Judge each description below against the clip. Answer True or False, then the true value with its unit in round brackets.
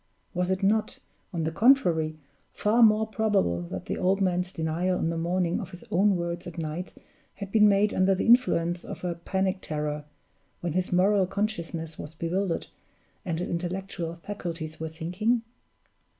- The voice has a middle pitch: True (180 Hz)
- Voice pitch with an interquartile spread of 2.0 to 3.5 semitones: True (3.1 semitones)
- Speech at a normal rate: True (165 wpm)